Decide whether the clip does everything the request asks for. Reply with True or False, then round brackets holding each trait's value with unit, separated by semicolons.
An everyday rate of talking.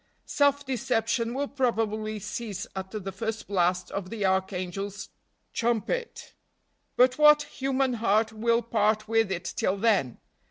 False (130 wpm)